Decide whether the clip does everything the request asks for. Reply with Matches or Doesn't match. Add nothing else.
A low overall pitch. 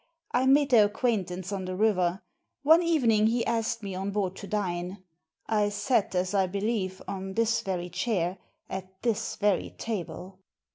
Doesn't match